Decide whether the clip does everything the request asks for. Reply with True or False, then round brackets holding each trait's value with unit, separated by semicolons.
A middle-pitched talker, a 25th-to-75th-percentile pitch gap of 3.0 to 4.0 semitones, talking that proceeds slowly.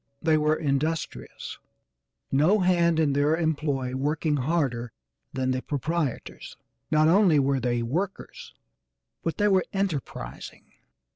True (155 Hz; 3.7 semitones; 120 wpm)